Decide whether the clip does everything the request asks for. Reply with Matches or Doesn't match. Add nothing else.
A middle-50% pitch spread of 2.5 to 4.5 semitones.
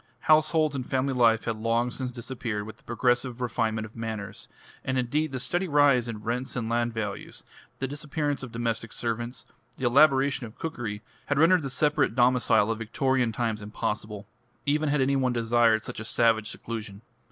Matches